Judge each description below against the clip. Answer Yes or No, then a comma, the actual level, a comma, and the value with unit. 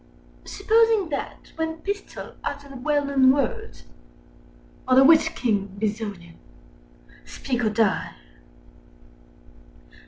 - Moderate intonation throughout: No, wide, 6.6 semitones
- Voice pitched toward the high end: Yes, very high, 270 Hz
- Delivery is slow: Yes, slow, 95 wpm